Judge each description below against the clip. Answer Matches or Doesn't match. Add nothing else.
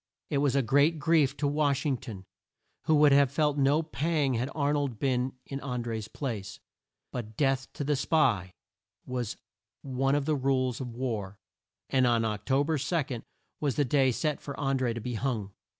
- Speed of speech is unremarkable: Matches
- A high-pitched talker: Doesn't match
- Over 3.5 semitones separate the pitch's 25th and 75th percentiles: Doesn't match